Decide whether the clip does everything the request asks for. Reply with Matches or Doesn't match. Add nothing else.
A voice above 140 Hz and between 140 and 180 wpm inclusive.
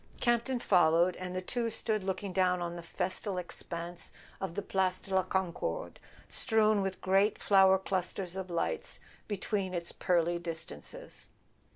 Matches